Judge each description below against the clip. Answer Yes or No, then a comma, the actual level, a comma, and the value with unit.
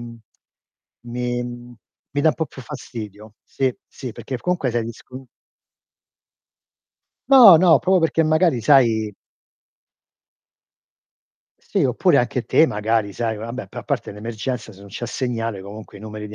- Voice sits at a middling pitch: No, low, 120 Hz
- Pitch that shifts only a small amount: No, average, 3.7 semitones